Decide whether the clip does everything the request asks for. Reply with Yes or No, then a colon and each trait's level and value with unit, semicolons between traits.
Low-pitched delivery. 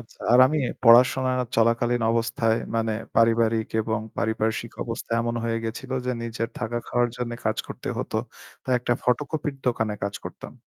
Yes: low, 115 Hz